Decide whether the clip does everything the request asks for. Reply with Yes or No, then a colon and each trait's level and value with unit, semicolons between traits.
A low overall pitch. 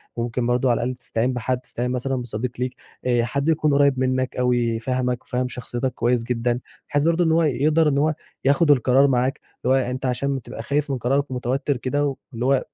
Yes: low, 130 Hz